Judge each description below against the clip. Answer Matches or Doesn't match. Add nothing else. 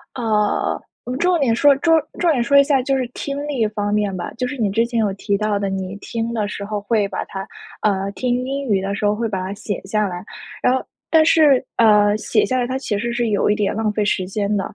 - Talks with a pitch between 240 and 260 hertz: Doesn't match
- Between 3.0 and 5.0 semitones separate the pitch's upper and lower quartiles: Matches